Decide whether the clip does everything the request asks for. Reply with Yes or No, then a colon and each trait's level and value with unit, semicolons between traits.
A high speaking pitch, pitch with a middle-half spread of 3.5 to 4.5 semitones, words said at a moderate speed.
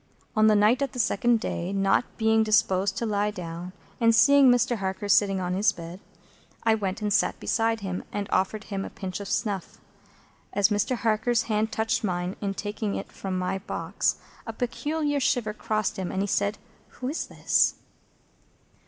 No: high, 210 Hz; average, 2.7 semitones; average, 180 wpm